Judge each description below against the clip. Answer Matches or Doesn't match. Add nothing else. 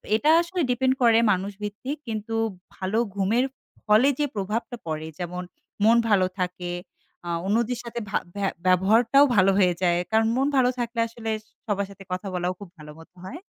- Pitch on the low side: Doesn't match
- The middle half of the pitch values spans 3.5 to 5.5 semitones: Matches